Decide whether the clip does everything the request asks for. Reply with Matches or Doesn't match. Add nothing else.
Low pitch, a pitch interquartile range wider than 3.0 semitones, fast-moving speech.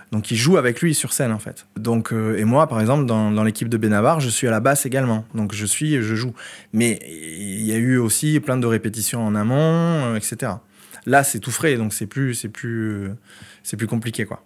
Matches